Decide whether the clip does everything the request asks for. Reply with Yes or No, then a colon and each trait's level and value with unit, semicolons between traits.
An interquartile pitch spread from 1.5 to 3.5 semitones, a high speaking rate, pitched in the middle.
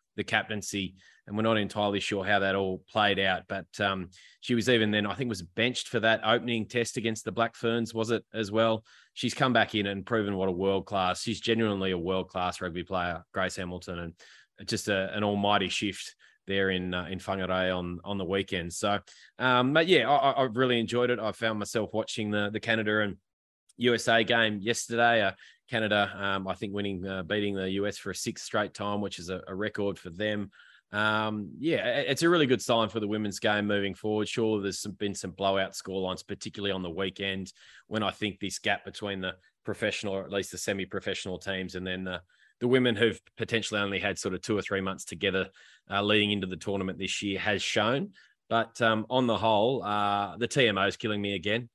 No: average, 2.7 semitones; fast, 215 wpm; low, 100 Hz